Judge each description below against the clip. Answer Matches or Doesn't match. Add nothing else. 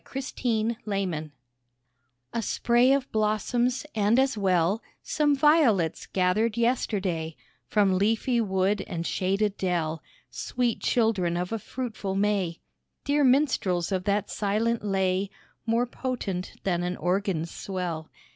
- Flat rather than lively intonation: Doesn't match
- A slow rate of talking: Matches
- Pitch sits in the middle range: Doesn't match